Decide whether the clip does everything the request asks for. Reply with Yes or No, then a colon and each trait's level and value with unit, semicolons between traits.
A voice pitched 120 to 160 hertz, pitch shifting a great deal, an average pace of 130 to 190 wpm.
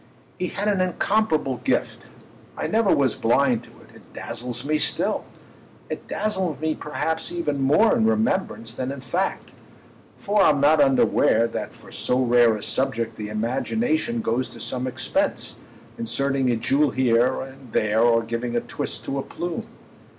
Yes: low, 135 Hz; wide, 6.4 semitones; average, 160 wpm